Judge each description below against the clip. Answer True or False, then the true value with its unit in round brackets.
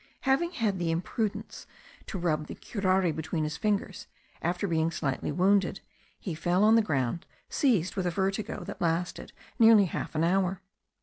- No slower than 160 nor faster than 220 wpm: True (165 wpm)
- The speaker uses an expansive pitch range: False (3.5 semitones)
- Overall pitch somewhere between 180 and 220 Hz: True (185 Hz)